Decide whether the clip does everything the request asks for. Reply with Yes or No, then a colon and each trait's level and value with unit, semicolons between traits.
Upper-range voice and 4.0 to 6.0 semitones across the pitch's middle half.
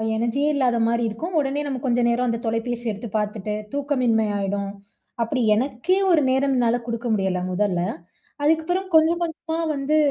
Yes: high, 245 Hz; average, 4.5 semitones